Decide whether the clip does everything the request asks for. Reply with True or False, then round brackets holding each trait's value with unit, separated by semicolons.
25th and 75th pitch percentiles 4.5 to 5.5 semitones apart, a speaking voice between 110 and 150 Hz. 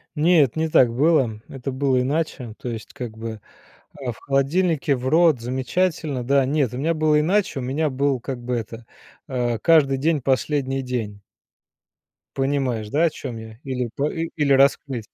False (3.6 semitones; 135 Hz)